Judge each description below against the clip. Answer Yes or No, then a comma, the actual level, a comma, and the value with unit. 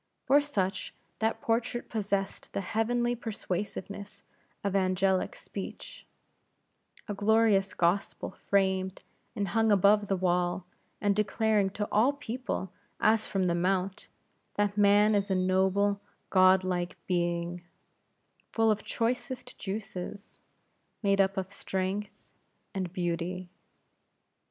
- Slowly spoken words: Yes, slow, 115 wpm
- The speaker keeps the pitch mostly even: Yes, narrow, 2.3 semitones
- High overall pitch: Yes, high, 200 Hz